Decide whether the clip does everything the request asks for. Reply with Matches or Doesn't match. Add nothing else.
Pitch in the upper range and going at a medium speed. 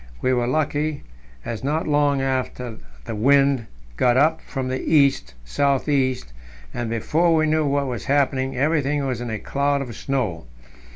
Doesn't match